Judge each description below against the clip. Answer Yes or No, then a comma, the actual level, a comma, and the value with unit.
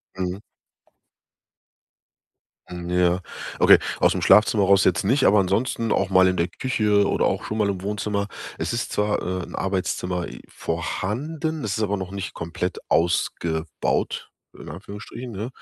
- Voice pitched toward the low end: Yes, very low, 95 Hz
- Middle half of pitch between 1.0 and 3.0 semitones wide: Yes, average, 2.7 semitones